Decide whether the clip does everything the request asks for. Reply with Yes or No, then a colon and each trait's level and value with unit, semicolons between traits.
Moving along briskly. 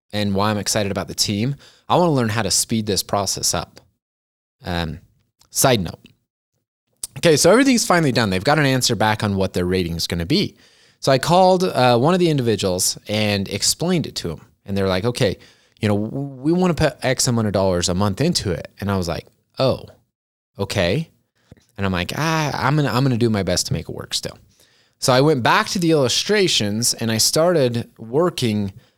Yes: fast, 215 wpm